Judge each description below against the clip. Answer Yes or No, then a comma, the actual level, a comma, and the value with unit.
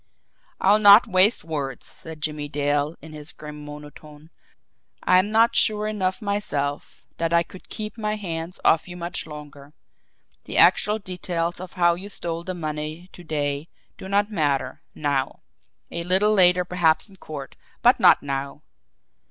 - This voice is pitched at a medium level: Yes, medium, 170 Hz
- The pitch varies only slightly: No, average, 4.3 semitones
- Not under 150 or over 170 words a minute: Yes, average, 155 wpm